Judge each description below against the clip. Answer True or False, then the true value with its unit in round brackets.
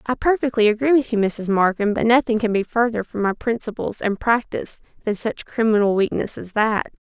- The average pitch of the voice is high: True (220 Hz)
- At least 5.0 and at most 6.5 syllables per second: True (5.5 syllables/s)